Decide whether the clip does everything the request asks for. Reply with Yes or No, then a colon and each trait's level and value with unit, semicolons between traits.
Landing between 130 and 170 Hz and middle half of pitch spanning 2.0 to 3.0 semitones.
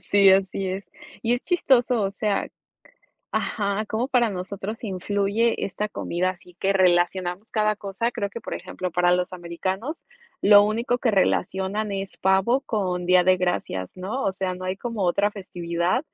No: high, 195 Hz; average, 2.7 semitones